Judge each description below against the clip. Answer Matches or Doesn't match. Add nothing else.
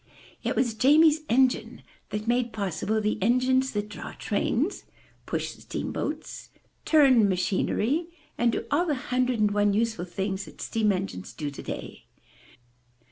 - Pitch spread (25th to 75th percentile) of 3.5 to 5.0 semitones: Matches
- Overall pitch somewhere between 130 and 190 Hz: Doesn't match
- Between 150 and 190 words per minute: Doesn't match